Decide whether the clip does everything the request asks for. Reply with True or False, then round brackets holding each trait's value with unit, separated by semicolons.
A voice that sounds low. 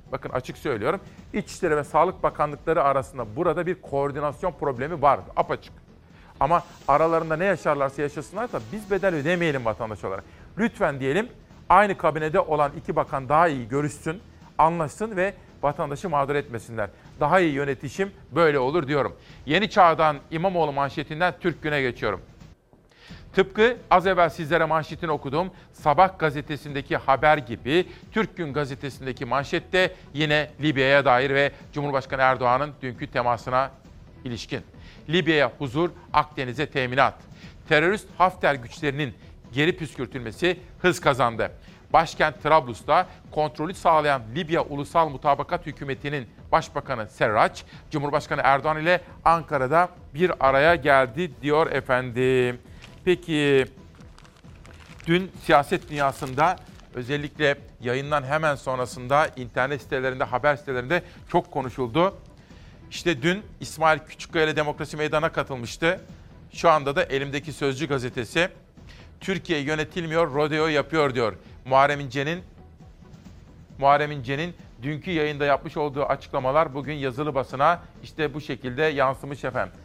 False (150 Hz)